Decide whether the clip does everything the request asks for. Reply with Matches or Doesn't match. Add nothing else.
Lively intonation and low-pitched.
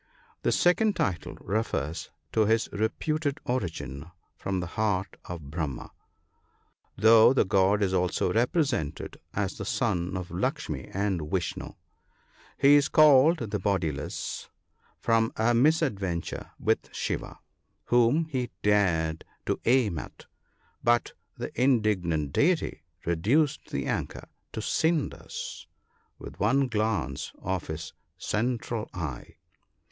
Matches